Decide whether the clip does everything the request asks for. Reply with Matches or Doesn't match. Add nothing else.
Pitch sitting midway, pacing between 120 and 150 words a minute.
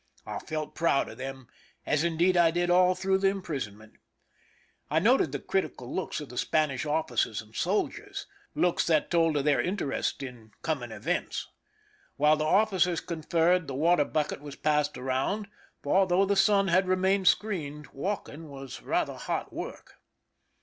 Doesn't match